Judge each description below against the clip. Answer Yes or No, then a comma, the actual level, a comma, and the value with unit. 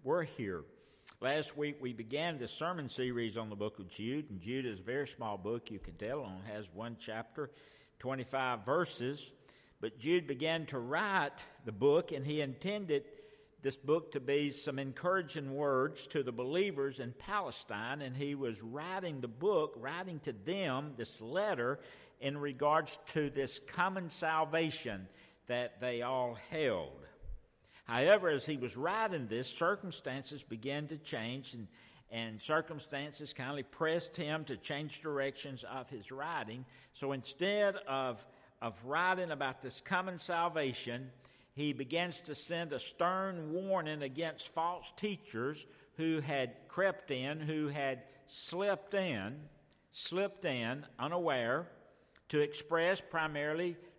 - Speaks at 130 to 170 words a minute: Yes, average, 145 wpm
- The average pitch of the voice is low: No, medium, 145 Hz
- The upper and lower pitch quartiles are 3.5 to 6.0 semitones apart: Yes, average, 4.4 semitones